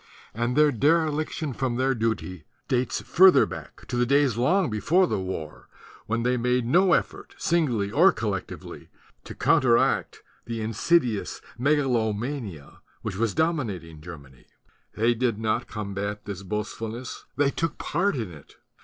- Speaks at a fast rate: No, average, 150 wpm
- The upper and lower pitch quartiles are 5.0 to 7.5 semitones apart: Yes, wide, 5.6 semitones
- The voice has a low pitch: Yes, low, 120 Hz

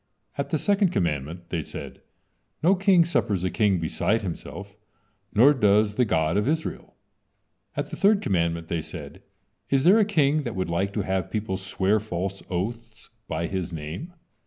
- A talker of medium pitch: No, low, 100 Hz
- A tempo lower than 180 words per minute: Yes, average, 170 wpm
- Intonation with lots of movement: Yes, wide, 7.9 semitones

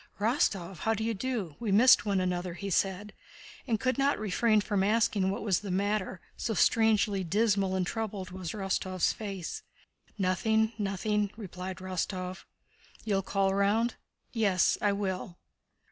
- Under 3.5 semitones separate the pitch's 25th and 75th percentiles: Yes, narrow, 2.6 semitones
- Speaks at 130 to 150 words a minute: Yes, average, 145 wpm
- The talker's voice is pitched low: No, high, 200 Hz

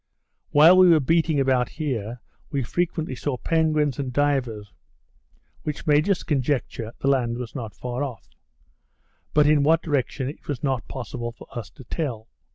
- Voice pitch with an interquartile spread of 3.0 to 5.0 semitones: Yes, average, 3.8 semitones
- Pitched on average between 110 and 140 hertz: Yes, low, 135 Hz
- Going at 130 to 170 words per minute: Yes, average, 165 wpm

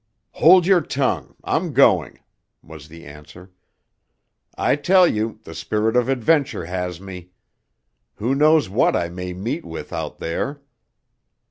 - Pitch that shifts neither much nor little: No, wide, 8.2 semitones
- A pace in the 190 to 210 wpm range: No, slow, 135 wpm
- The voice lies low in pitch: Yes, low, 110 Hz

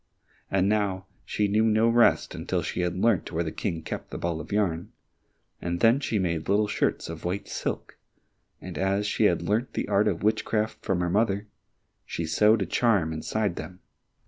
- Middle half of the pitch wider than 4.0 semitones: No, average, 3.5 semitones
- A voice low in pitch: Yes, low, 100 Hz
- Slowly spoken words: No, average, 190 wpm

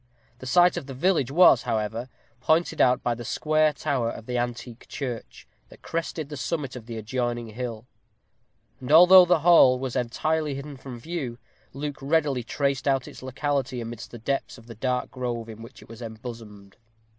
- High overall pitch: No, low, 130 Hz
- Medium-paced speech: Yes, average, 180 wpm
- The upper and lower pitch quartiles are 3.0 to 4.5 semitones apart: Yes, average, 3.7 semitones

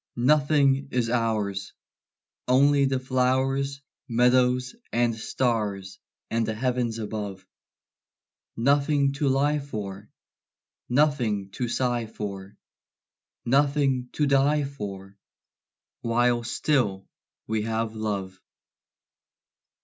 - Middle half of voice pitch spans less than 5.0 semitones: Yes, average, 4.1 semitones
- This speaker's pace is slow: Yes, slow, 90 wpm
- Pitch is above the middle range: No, low, 120 Hz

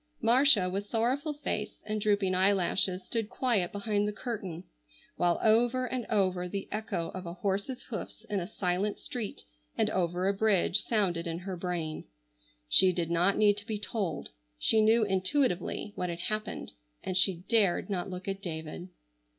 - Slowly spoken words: No, average, 165 wpm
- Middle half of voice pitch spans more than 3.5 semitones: No, average, 3.2 semitones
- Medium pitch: No, high, 195 Hz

